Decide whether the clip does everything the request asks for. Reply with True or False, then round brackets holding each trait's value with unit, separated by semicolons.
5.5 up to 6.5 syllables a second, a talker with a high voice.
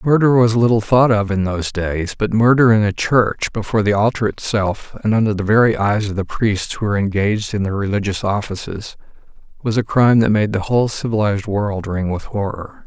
False (5.6 syllables/s; 105 Hz)